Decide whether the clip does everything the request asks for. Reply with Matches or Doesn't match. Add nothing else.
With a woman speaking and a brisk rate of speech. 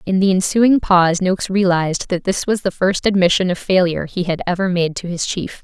Matches